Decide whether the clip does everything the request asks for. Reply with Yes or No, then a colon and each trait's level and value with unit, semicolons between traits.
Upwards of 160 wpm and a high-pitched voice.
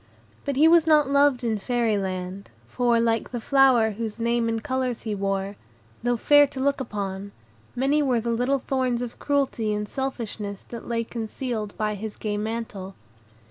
Yes: average, 175 wpm; high, 235 Hz